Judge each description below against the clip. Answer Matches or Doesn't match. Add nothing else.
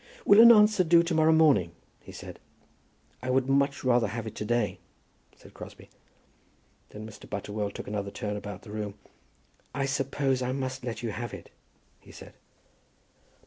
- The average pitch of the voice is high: Doesn't match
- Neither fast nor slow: Matches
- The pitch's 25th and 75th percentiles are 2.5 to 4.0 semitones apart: Doesn't match